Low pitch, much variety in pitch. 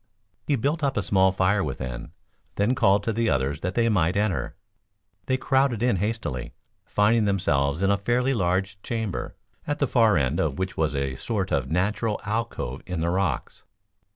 Yes: low, 100 Hz; wide, 6.2 semitones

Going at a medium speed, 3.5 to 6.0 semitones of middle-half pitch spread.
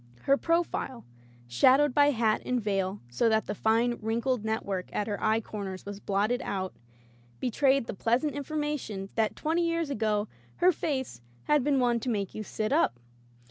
Yes: average, 170 wpm; average, 5.0 semitones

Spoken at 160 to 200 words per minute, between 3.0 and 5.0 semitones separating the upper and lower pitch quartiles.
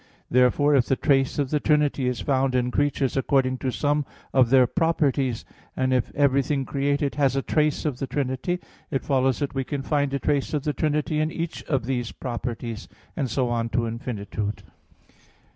No: average, 185 wpm; narrow, 2.4 semitones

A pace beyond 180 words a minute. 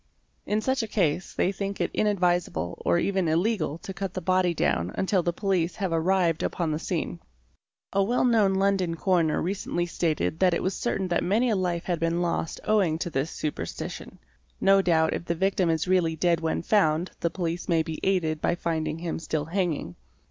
Yes: average, 195 wpm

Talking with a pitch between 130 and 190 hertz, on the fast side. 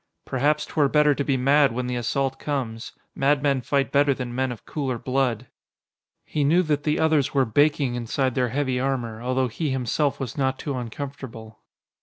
No: low, 135 Hz; average, 180 wpm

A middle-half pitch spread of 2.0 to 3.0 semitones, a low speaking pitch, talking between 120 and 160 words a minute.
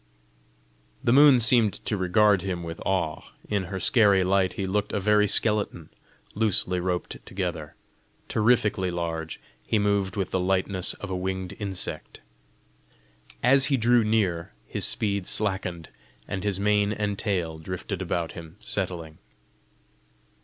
Yes: average, 2.7 semitones; very low, 95 Hz; average, 140 wpm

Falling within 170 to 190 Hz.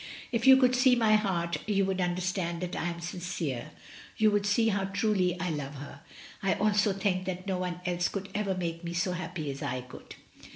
Yes: medium, 185 Hz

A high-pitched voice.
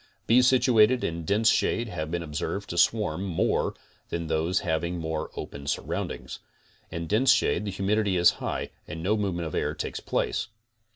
No: very low, 90 Hz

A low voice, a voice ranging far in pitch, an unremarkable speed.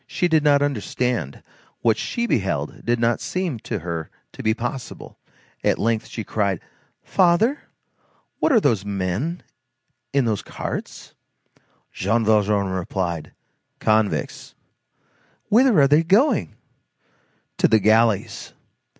No: low, 115 Hz; wide, 6.8 semitones; slow, 120 wpm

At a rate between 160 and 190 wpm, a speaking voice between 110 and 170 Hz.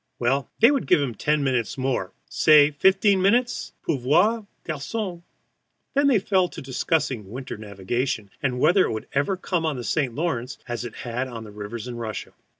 Yes: average, 175 wpm; low, 135 Hz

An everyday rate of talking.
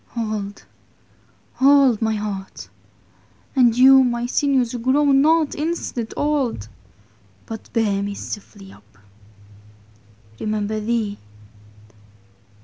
No: slow, 95 wpm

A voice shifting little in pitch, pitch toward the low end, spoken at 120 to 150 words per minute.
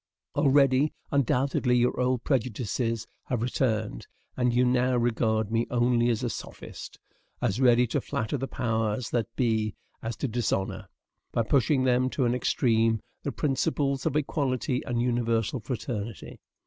Yes: narrow, 2.3 semitones; low, 120 Hz; average, 145 wpm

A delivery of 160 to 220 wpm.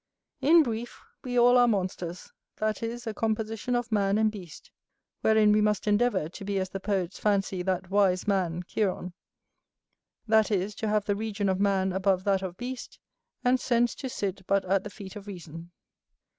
Yes: average, 185 wpm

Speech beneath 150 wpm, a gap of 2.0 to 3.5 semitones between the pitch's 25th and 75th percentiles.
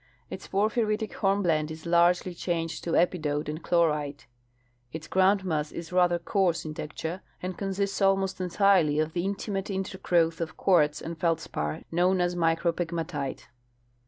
Yes: average, 140 wpm; average, 3.1 semitones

